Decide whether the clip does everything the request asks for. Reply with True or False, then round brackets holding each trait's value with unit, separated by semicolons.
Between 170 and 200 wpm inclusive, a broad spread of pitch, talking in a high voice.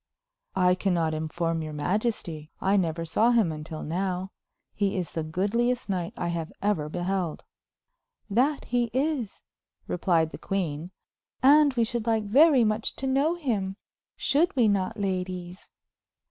False (145 wpm; 5.7 semitones; 195 Hz)